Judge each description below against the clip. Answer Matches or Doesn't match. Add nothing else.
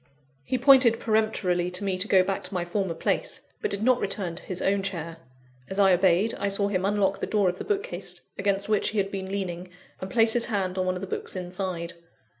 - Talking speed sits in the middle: Doesn't match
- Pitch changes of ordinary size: Doesn't match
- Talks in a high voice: Matches